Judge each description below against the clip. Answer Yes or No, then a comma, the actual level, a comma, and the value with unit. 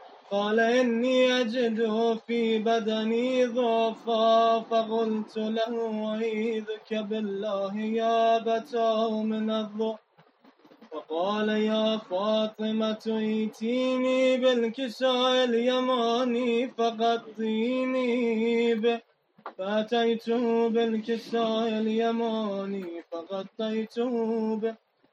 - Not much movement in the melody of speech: Yes, narrow, 1.2 semitones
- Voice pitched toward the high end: Yes, high, 225 Hz